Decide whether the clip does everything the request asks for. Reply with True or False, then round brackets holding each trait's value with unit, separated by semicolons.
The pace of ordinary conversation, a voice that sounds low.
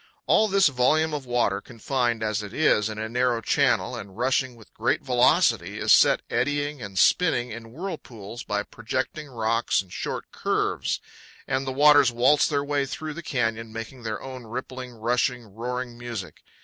True (170 wpm; 125 Hz)